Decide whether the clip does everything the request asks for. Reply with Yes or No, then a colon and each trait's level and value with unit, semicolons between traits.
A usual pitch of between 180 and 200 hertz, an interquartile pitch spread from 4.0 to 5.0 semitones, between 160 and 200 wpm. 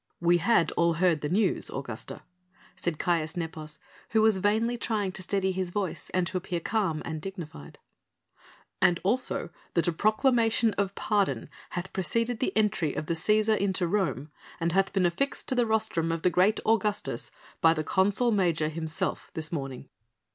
Yes: medium, 185 Hz; average, 4.3 semitones; average, 170 wpm